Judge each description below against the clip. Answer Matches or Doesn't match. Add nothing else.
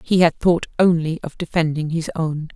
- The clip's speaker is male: Doesn't match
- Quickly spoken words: Doesn't match